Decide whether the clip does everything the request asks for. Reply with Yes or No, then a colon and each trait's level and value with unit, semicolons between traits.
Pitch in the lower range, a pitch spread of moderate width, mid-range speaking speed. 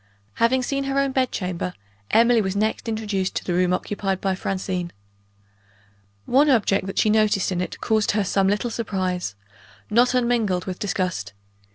No: high, 205 Hz; average, 3.8 semitones; average, 165 wpm